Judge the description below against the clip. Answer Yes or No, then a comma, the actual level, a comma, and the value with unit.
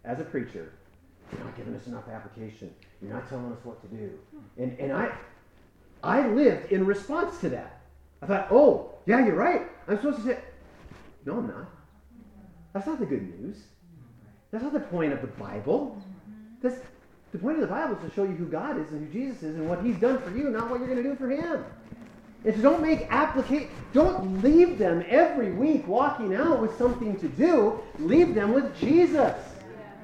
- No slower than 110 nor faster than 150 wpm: No, average, 200 wpm